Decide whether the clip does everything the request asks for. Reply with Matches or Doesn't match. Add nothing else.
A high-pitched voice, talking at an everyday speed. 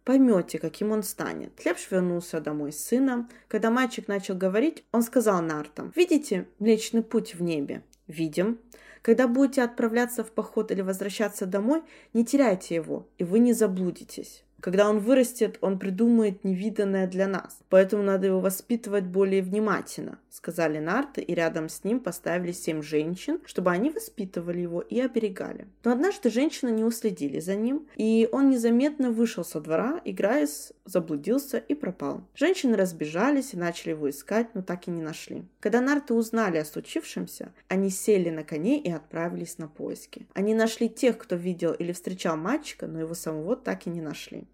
Doesn't match